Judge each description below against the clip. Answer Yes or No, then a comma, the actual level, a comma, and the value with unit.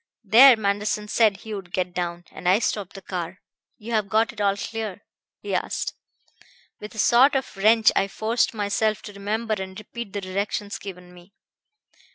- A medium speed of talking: Yes, average, 175 wpm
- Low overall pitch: No, high, 205 Hz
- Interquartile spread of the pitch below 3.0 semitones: Yes, narrow, 2.5 semitones